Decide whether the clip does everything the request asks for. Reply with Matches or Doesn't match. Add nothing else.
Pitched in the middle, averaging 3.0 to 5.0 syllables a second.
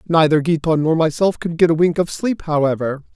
Doesn't match